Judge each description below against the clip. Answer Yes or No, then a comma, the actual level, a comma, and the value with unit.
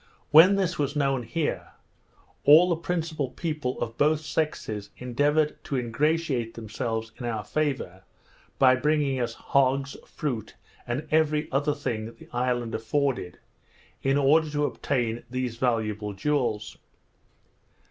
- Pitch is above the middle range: No, low, 135 Hz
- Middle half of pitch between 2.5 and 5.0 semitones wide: Yes, average, 4.5 semitones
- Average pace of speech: No, slow, 125 wpm